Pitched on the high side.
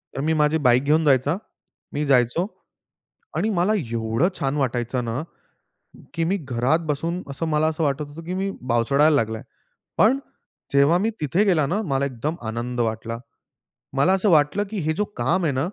No: medium, 145 Hz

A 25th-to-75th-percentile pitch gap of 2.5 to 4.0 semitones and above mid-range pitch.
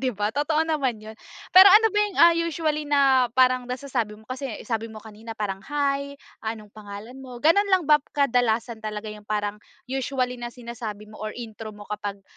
No: average, 4.7 semitones; high, 245 Hz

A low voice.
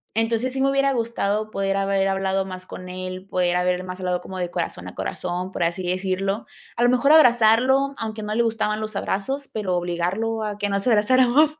No: high, 200 Hz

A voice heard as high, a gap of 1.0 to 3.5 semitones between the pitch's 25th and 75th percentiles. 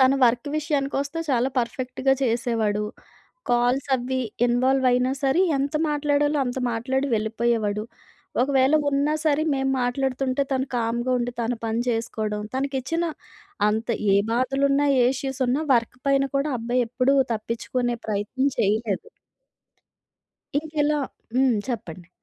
Yes: very high, 255 Hz; average, 2.9 semitones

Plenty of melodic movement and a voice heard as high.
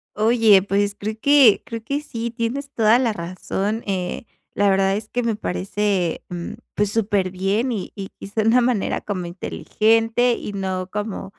No: average, 3.0 semitones; high, 210 Hz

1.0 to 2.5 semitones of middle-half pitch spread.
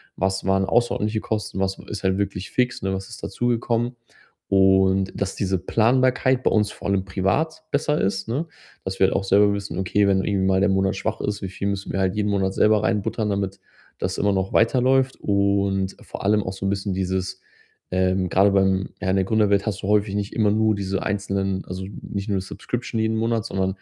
Yes: narrow, 2.1 semitones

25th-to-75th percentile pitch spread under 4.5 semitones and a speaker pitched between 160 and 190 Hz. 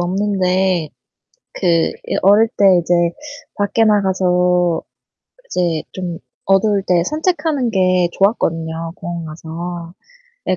Yes: average, 2.9 semitones; medium, 185 Hz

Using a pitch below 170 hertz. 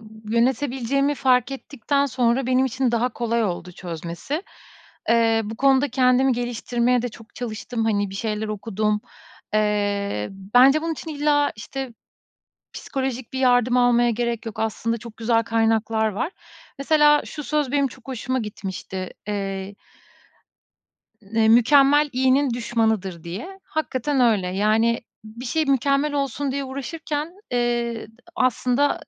No: high, 240 Hz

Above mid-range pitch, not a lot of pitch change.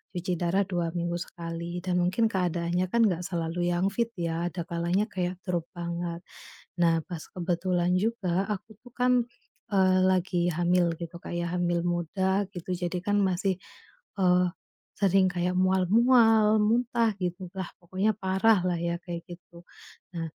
No: medium, 180 Hz; narrow, 1.8 semitones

